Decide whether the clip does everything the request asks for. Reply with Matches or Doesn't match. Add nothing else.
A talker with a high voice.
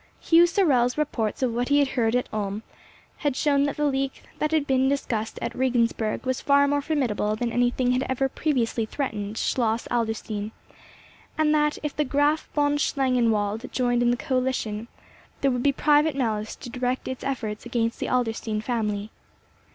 Matches